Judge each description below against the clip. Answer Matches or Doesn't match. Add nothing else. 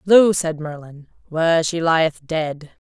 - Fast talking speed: Doesn't match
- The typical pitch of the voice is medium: Matches